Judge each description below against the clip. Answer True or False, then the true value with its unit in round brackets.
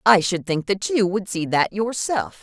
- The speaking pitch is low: False (190 Hz)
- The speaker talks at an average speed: False (220 wpm)